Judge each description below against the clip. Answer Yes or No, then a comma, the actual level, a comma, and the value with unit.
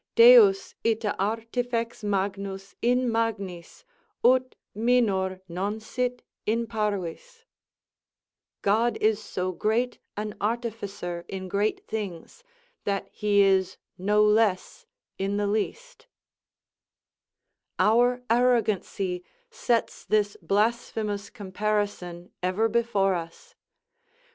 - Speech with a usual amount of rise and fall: Yes, average, 3.1 semitones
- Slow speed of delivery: Yes, slow, 95 wpm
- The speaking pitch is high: Yes, high, 210 Hz